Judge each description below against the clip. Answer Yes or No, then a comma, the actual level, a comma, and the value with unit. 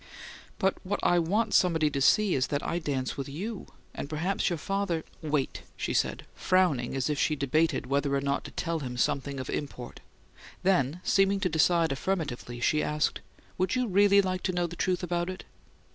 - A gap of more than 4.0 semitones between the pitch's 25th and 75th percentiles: Yes, average, 5.0 semitones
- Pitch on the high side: No, medium, 165 Hz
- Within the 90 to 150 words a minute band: No, average, 195 wpm